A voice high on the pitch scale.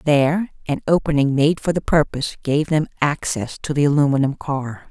No: medium, 145 Hz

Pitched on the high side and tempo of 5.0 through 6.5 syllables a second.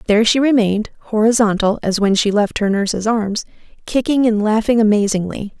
Yes: high, 215 Hz; 5.7 syllables/s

